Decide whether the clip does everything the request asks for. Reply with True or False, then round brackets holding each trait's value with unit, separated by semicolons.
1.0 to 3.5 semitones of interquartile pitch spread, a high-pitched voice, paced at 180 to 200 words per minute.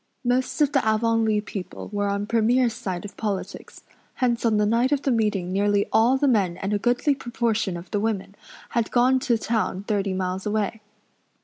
True (3.1 semitones; 220 Hz; 190 wpm)